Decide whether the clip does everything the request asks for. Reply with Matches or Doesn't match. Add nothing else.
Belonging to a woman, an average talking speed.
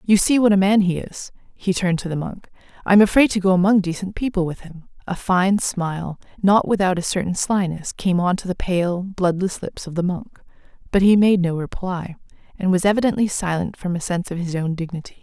Doesn't match